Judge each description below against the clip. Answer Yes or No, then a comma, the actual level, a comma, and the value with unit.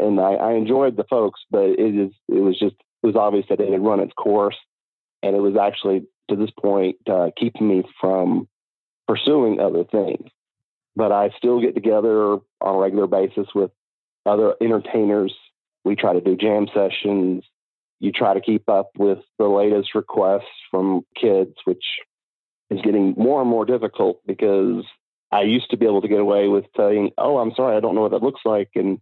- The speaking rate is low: No, average, 190 wpm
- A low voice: Yes, low, 100 Hz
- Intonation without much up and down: Yes, narrow, 1.8 semitones